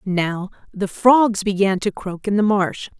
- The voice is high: Yes, high, 200 Hz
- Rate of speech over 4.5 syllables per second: No, 3.9 syllables/s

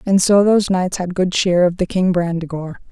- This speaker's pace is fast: Yes, fast, 225 wpm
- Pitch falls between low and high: Yes, medium, 180 Hz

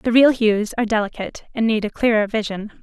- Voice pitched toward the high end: Yes, high, 220 Hz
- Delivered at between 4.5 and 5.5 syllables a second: No, 6.0 syllables/s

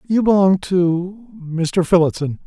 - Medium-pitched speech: Yes, medium, 180 Hz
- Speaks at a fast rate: No, slow, 95 wpm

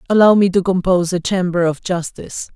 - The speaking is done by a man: Yes, male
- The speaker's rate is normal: Yes, average, 190 wpm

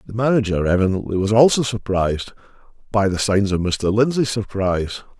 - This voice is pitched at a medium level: No, low, 105 Hz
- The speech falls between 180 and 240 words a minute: No, average, 140 wpm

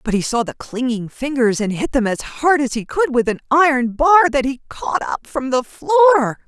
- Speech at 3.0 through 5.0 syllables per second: Yes, 4.9 syllables/s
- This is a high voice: Yes, very high, 270 Hz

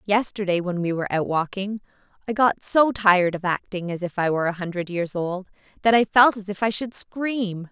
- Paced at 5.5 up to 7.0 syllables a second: No, 5.3 syllables/s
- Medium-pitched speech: No, high, 195 Hz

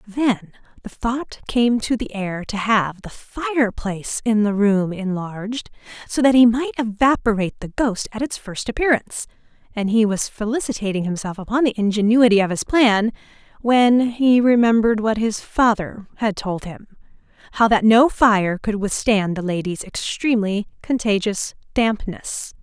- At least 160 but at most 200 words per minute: No, average, 150 wpm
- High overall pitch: Yes, high, 220 Hz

